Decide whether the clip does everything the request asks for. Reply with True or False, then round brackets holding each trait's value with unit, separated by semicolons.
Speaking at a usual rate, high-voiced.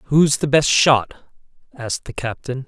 False (155 wpm; 135 Hz)